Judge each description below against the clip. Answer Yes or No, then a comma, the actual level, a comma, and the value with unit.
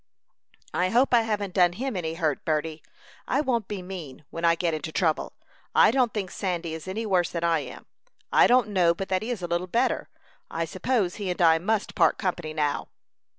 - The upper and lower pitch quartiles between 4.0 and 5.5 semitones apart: Yes, average, 4.3 semitones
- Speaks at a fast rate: Yes, fast, 210 wpm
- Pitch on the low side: No, medium, 180 Hz